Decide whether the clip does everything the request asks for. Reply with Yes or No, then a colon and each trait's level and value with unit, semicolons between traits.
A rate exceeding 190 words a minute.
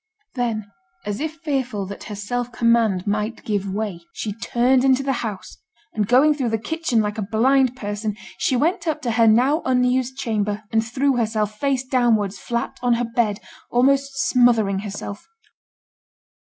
No: average, 165 wpm